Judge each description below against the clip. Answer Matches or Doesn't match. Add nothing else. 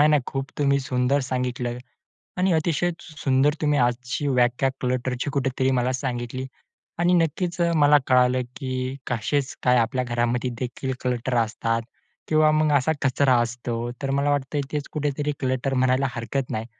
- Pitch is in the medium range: Doesn't match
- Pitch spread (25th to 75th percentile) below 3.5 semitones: Matches